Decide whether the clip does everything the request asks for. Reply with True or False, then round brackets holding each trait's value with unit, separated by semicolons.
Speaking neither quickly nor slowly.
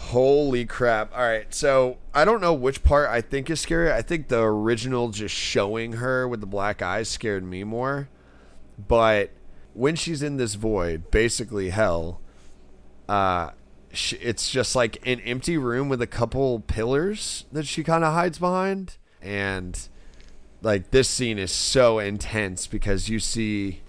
True (160 wpm)